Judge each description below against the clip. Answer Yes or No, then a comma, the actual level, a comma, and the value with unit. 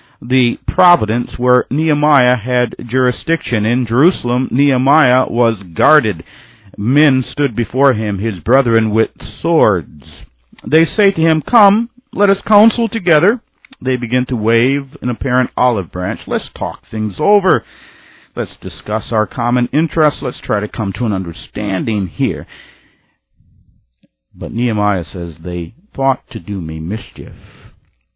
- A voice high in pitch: No, low, 125 Hz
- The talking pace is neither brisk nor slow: No, slow, 130 wpm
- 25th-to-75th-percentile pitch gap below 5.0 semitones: No, average, 5.3 semitones